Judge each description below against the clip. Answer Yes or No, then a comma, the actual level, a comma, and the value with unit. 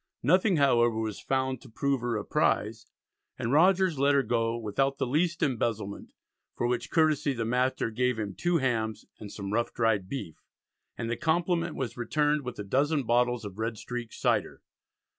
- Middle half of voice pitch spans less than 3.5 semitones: No, average, 4.0 semitones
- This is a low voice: Yes, low, 125 Hz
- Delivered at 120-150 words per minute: No, average, 180 wpm